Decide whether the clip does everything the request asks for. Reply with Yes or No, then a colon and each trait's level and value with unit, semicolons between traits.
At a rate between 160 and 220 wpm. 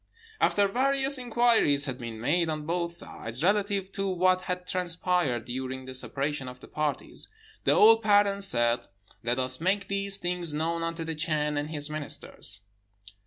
Yes: average, 165 wpm